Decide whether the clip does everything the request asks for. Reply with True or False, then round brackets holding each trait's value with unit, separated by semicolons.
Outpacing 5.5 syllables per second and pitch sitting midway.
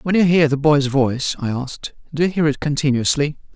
True (5.8 syllables/s; 145 Hz)